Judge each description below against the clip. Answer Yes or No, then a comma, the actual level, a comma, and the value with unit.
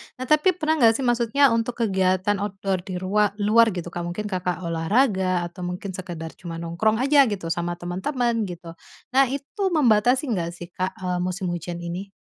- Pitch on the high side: Yes, high, 195 Hz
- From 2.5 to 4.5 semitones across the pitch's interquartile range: No, average, 5.0 semitones